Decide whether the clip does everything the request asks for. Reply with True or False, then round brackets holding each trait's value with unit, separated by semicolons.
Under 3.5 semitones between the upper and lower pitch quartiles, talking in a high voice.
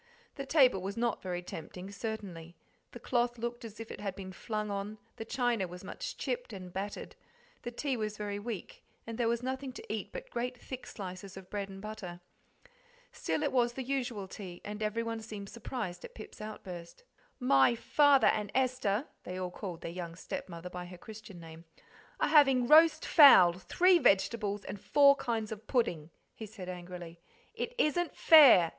False (5.0 semitones; 215 Hz)